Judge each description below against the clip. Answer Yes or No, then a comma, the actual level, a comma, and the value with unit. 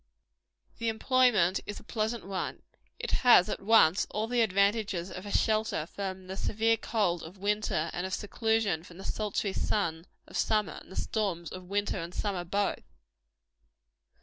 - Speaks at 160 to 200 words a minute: Yes, average, 170 wpm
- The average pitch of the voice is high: Yes, high, 200 Hz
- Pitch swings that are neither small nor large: Yes, average, 3.2 semitones